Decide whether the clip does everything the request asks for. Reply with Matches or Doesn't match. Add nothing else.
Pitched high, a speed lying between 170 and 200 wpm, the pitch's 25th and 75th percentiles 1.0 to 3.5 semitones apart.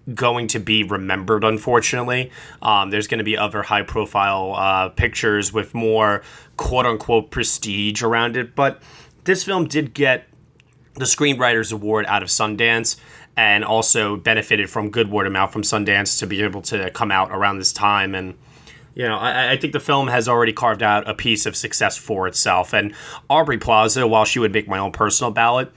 Doesn't match